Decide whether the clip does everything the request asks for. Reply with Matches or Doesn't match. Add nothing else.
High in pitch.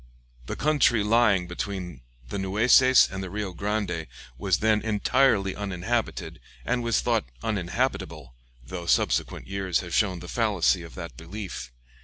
Doesn't match